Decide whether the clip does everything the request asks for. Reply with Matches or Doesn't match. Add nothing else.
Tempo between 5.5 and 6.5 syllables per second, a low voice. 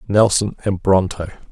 Doesn't match